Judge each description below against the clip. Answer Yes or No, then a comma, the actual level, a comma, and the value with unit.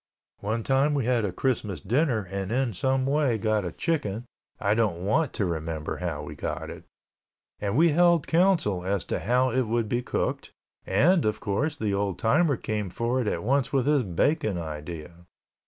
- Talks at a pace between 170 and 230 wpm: Yes, average, 185 wpm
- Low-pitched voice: Yes, low, 115 Hz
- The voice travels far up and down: Yes, wide, 5.9 semitones